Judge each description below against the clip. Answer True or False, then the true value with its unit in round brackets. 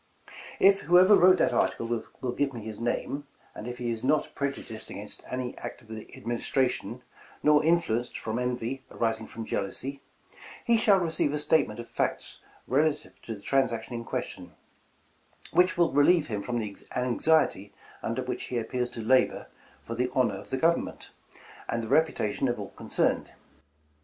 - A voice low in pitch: True (125 Hz)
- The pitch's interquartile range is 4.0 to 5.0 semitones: True (4.5 semitones)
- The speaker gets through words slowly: False (175 wpm)